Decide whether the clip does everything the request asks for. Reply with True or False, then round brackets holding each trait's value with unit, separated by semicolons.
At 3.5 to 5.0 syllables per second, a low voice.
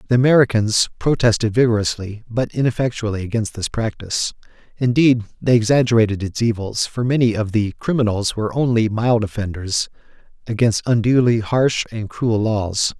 False (5.3 syllables/s; 115 Hz)